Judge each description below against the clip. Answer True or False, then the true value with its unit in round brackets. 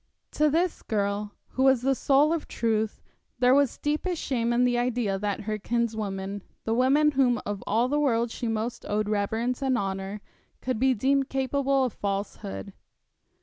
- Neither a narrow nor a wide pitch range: True (4.2 semitones)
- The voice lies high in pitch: True (240 Hz)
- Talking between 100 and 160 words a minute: False (170 wpm)